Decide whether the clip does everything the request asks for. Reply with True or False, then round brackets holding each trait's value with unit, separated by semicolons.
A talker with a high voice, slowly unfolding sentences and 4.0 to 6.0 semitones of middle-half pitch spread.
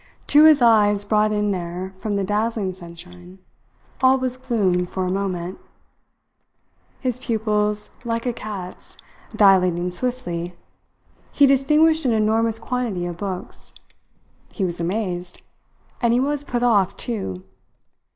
True (210 Hz; 130 wpm; 4.8 semitones)